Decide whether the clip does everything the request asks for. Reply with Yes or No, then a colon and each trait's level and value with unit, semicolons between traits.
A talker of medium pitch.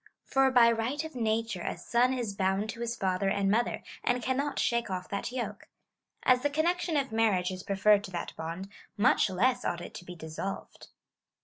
No: high, 225 Hz